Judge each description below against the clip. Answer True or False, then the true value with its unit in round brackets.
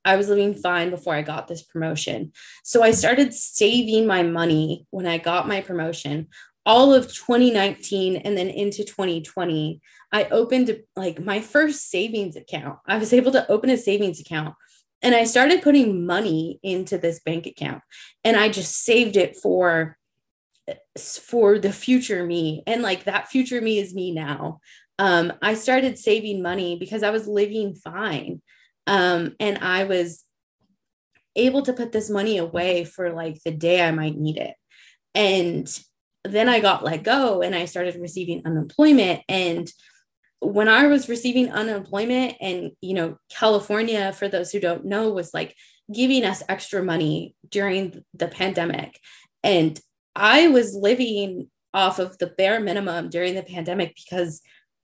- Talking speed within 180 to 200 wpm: False (160 wpm)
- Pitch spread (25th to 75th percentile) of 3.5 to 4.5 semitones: True (4.1 semitones)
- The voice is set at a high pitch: True (195 Hz)